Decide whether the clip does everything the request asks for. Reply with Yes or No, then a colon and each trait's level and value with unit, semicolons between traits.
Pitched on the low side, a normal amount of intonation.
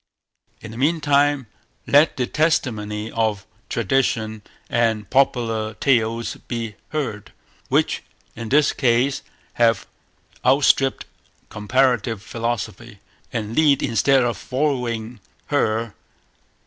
Yes: low, 120 Hz; average, 3.5 semitones